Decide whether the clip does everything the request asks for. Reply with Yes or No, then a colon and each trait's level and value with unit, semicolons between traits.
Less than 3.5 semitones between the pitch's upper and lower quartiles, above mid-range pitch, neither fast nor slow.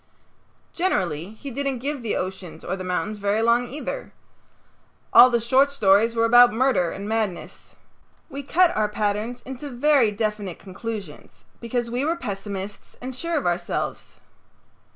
No: average, 4.5 semitones; high, 230 Hz; average, 150 wpm